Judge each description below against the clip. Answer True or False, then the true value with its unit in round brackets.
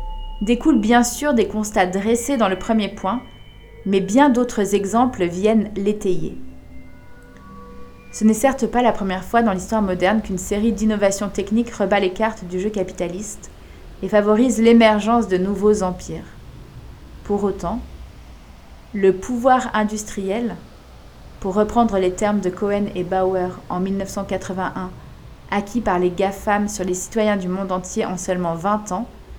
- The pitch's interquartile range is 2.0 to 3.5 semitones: True (3.0 semitones)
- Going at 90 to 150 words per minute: True (145 wpm)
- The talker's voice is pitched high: True (205 Hz)